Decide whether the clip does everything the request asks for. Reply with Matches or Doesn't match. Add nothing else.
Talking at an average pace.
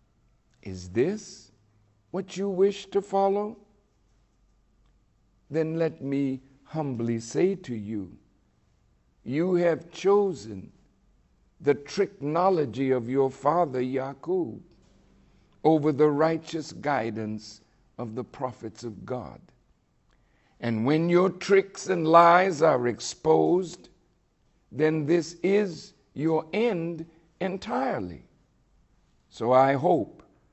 Doesn't match